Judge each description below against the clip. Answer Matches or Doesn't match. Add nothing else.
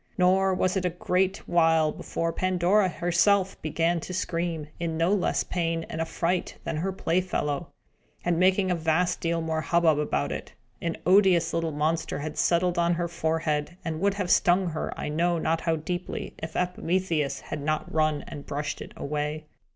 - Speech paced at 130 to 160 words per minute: Doesn't match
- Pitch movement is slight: Matches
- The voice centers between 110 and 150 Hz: Doesn't match